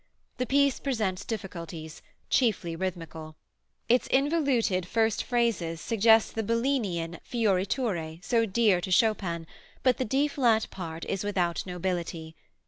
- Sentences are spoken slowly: Yes, slow, 130 wpm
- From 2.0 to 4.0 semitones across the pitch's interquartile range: No, wide, 5.5 semitones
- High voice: Yes, high, 205 Hz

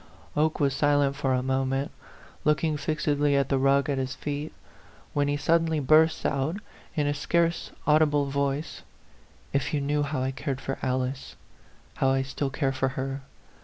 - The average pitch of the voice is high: No, medium, 140 Hz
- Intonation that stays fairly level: Yes, narrow, 1.9 semitones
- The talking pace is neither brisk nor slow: Yes, average, 175 wpm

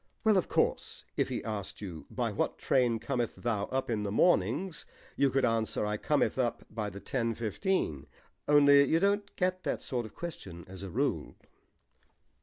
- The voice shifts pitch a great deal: Yes, wide, 6.1 semitones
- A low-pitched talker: Yes, low, 120 Hz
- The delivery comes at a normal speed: Yes, average, 180 wpm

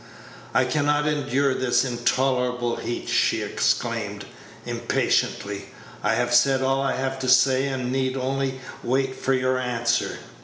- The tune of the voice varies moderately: No, narrow, 1.3 semitones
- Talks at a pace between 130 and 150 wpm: Yes, average, 145 wpm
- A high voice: No, low, 130 Hz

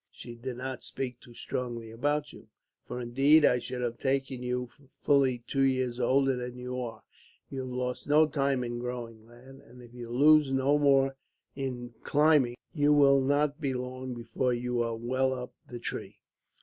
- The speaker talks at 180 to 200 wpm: Yes, average, 185 wpm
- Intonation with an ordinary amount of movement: No, narrow, 2.0 semitones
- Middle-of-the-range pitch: No, low, 130 Hz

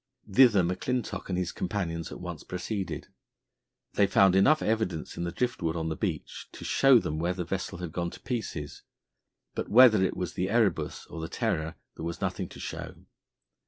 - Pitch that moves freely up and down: No, average, 4.2 semitones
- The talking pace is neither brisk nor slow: Yes, average, 190 wpm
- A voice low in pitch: Yes, very low, 90 Hz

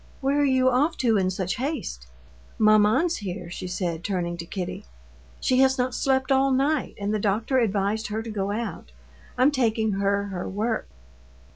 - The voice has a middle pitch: No, high, 220 Hz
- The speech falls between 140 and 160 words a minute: No, average, 175 wpm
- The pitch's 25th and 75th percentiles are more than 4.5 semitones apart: Yes, average, 4.9 semitones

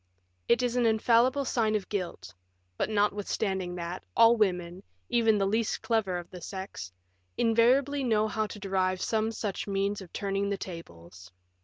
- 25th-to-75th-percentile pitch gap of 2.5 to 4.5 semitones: Yes, average, 3.4 semitones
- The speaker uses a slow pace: No, average, 160 wpm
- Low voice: No, high, 205 Hz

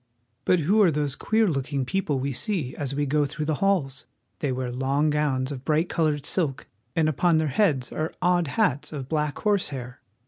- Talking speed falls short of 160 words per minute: No, average, 195 wpm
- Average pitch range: Yes, average, 3.5 semitones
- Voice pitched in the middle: Yes, medium, 150 Hz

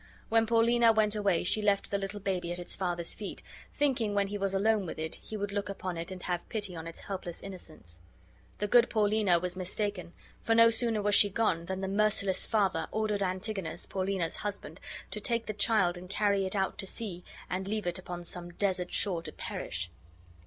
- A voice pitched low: No, high, 195 Hz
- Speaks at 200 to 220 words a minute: Yes, fast, 205 wpm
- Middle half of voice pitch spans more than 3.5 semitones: No, average, 3.0 semitones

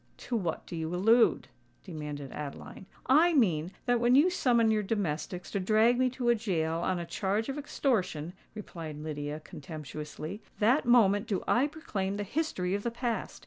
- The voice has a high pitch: Yes, high, 200 Hz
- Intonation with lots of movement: Yes, wide, 6.7 semitones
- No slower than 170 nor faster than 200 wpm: Yes, average, 175 wpm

